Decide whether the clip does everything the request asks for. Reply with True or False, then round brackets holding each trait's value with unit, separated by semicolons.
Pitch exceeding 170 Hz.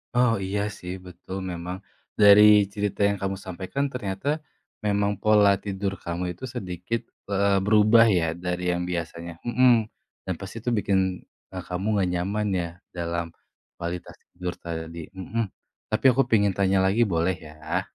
False (95 Hz)